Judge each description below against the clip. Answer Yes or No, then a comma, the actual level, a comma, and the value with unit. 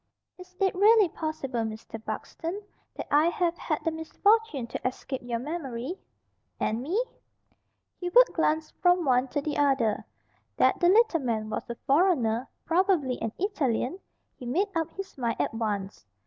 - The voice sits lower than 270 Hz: No, very high, 305 Hz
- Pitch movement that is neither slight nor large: No, wide, 6.9 semitones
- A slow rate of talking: No, average, 155 wpm